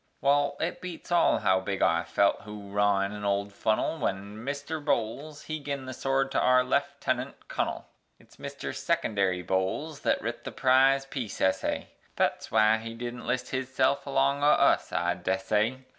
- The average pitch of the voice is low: Yes, low, 125 Hz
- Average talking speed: Yes, average, 165 wpm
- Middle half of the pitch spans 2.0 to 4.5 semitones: No, average, 5.3 semitones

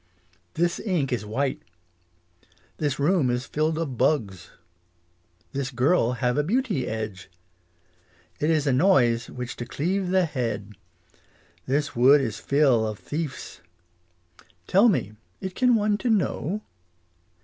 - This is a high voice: No, medium, 140 Hz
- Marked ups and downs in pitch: Yes, wide, 6.4 semitones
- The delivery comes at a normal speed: No, slow, 130 wpm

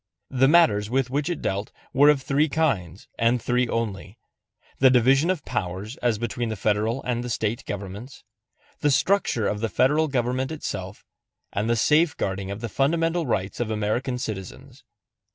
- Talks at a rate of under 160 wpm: No, average, 165 wpm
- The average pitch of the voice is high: No, low, 120 Hz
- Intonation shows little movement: No, average, 4.7 semitones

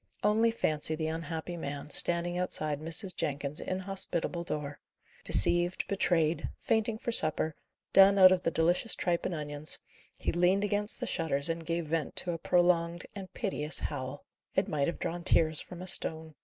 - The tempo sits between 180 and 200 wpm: No, average, 170 wpm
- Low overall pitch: No, medium, 170 Hz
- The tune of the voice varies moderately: Yes, average, 3.0 semitones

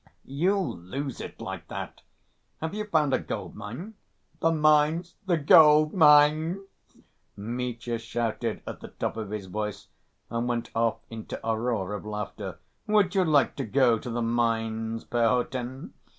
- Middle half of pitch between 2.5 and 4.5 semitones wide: No, average, 5.3 semitones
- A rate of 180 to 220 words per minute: No, average, 145 wpm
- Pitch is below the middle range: Yes, low, 125 Hz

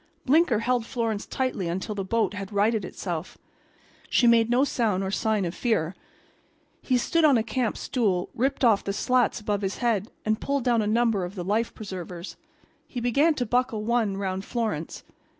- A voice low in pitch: No, high, 220 Hz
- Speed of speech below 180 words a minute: No, average, 185 wpm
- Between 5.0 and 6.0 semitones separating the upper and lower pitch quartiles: No, average, 3.7 semitones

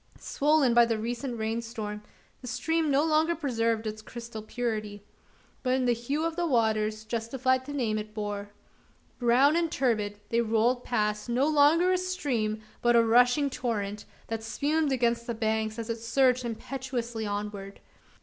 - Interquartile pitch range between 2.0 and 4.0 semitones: Yes, average, 3.6 semitones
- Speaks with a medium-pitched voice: No, high, 235 Hz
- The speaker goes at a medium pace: Yes, average, 165 wpm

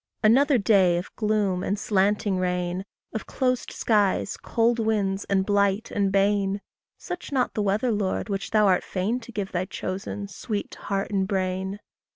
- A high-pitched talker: Yes, high, 200 Hz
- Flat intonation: Yes, narrow, 2.2 semitones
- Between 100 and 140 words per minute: No, average, 170 wpm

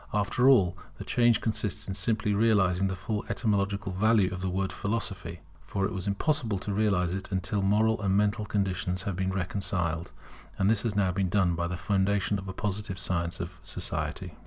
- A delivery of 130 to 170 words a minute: No, average, 190 wpm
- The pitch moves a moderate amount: No, narrow, 2.2 semitones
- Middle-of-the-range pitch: No, low, 100 Hz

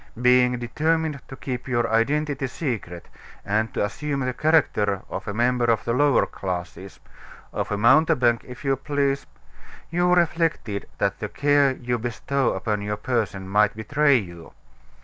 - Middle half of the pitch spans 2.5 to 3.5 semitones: No, average, 5.3 semitones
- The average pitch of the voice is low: Yes, low, 125 Hz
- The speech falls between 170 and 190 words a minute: No, average, 150 wpm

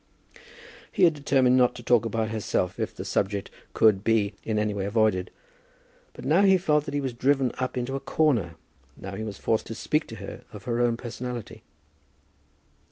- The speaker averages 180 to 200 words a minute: Yes, average, 190 wpm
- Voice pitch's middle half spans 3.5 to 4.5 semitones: Yes, average, 4.0 semitones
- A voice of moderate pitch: No, low, 115 Hz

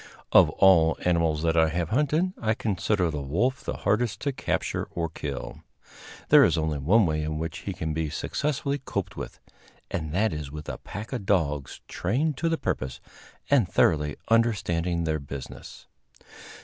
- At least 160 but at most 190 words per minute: Yes, average, 170 wpm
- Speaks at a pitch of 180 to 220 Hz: No, very low, 85 Hz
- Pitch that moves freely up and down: Yes, wide, 6.4 semitones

